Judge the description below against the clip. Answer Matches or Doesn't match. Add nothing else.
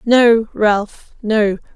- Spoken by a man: Doesn't match